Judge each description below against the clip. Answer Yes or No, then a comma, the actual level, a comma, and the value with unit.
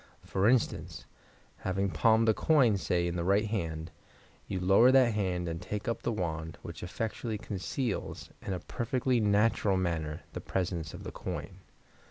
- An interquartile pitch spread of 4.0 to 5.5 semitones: Yes, average, 4.3 semitones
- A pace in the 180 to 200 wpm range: No, average, 165 wpm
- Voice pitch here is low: Yes, low, 100 Hz